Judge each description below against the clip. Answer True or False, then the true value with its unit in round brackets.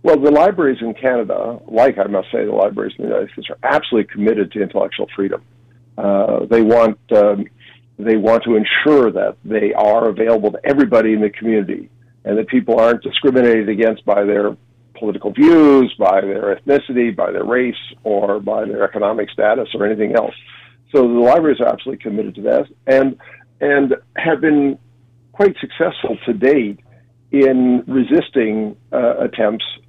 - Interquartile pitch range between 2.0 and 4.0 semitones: True (2.9 semitones)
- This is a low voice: True (120 Hz)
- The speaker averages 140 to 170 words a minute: True (165 wpm)